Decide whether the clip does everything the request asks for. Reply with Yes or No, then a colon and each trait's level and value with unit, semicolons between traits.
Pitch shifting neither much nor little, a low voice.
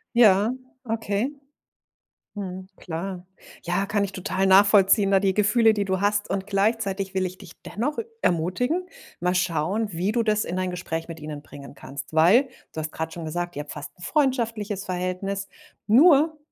No: average, 3.2 semitones; high, 195 Hz